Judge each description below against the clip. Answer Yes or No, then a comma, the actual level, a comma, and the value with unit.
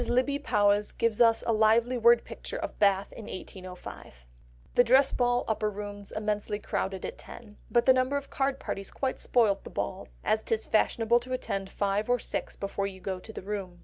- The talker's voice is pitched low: No, high, 215 Hz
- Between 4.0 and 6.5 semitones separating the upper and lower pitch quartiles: No, average, 3.4 semitones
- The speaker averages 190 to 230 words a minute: Yes, average, 195 wpm